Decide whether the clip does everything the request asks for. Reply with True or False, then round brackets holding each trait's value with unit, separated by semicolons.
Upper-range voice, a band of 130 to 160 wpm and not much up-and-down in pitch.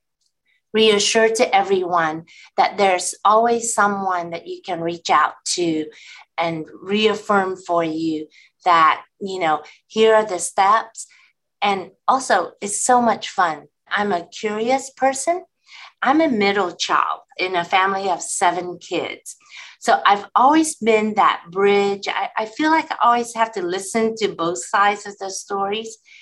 False (200 Hz; 150 wpm; 4.0 semitones)